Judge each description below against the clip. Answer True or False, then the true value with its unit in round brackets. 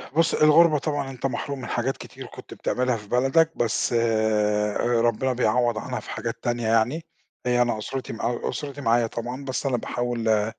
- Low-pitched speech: True (120 Hz)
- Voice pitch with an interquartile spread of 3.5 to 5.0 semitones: False (2.9 semitones)